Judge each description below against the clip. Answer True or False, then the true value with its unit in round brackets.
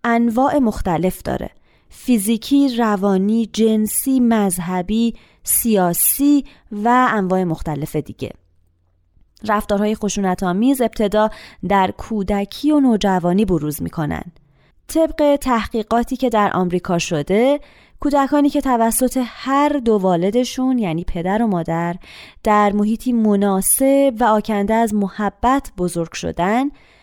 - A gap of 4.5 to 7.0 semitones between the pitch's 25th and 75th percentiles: True (5.2 semitones)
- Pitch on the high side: True (215 Hz)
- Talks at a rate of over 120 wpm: False (105 wpm)